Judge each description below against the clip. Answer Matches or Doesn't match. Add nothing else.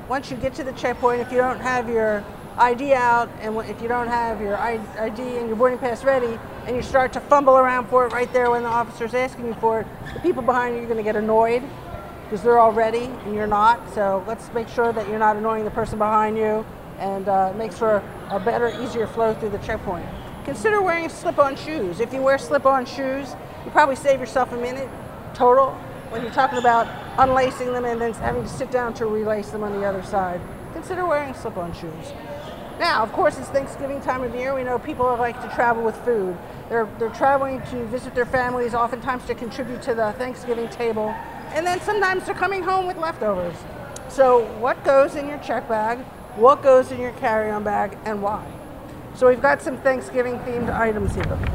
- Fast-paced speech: Matches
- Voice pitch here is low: Doesn't match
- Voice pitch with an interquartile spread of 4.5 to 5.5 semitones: Doesn't match